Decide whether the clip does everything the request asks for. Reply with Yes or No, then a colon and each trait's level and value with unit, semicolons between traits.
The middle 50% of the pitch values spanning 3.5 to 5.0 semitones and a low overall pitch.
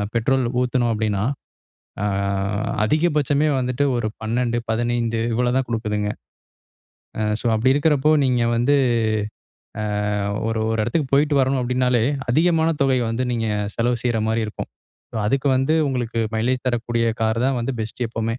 No: average, 2.8 semitones; low, 120 Hz